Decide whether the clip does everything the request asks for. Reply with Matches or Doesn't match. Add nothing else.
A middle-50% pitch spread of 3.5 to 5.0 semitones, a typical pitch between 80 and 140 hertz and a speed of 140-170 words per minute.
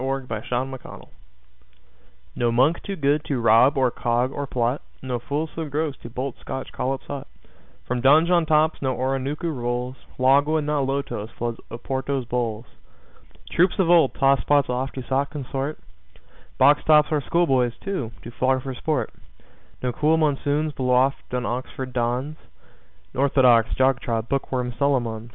Doesn't match